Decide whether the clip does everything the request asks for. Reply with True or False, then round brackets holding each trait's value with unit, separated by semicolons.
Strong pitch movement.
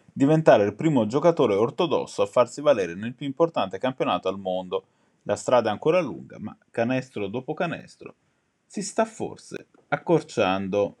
True (8.4 semitones)